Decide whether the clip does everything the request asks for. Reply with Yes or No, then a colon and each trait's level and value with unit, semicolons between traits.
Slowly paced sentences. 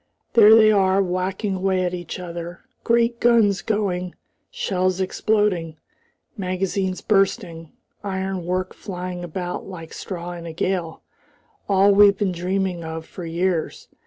Yes: slow, 130 wpm